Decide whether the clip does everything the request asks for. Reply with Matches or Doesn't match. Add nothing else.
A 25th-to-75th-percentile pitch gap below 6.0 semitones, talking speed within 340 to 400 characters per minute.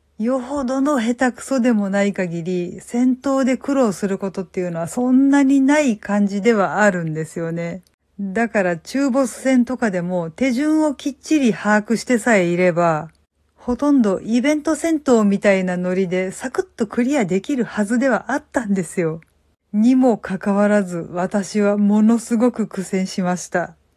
Doesn't match